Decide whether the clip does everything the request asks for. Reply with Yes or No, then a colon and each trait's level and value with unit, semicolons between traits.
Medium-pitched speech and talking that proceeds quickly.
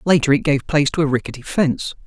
Yes: medium, 145 Hz; fast, 230 wpm